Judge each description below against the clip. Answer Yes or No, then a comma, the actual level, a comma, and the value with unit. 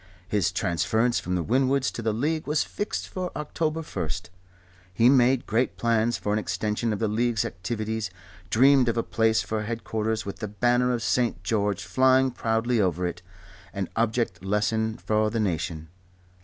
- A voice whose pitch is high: No, low, 110 Hz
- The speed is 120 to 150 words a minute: No, average, 170 wpm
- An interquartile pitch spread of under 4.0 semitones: Yes, average, 2.8 semitones